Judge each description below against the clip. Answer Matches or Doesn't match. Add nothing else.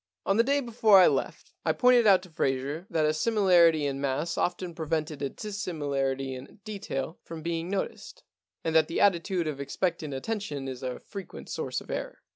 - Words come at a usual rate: Matches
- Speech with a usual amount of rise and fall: Doesn't match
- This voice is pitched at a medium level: Matches